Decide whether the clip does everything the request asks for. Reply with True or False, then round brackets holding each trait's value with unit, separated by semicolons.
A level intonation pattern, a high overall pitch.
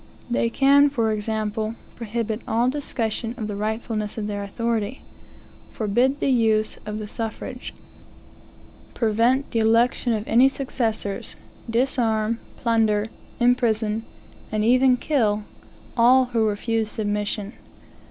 True (2.3 semitones; 225 Hz)